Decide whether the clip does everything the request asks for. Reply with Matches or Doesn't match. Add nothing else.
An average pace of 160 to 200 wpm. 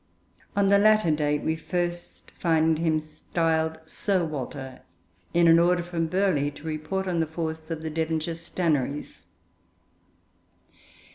Doesn't match